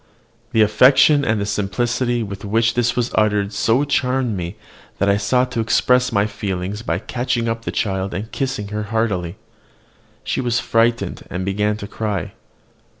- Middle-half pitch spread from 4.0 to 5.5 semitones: No, average, 3.2 semitones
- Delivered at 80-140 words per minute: No, average, 160 wpm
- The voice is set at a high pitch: No, low, 110 Hz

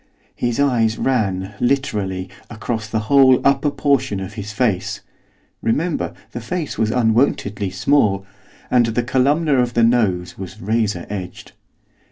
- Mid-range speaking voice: No, low, 115 Hz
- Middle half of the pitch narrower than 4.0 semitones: No, average, 4.3 semitones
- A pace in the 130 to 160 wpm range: Yes, average, 145 wpm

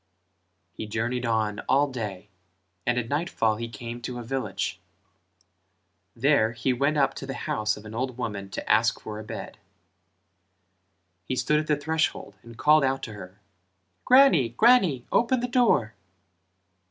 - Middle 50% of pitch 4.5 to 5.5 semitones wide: Yes, average, 4.8 semitones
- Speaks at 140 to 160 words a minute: Yes, average, 155 wpm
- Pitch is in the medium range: No, low, 120 Hz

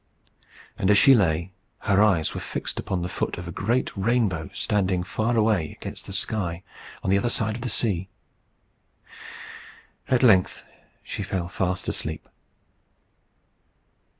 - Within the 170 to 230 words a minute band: No, average, 145 wpm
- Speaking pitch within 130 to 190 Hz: No, very low, 95 Hz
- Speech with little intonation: No, average, 3.6 semitones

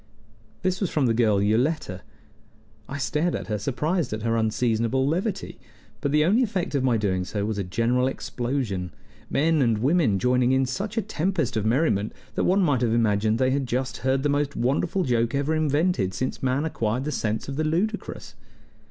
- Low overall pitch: Yes, low, 130 Hz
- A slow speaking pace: No, average, 190 wpm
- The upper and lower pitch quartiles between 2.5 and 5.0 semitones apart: No, wide, 5.4 semitones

